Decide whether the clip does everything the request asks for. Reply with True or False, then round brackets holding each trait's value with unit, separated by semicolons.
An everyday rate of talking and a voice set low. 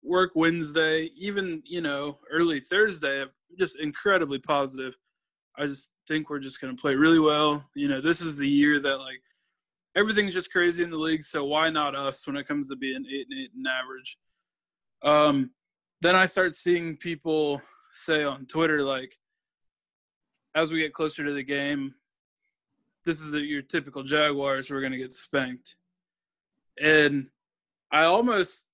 False (165 wpm; 150 Hz)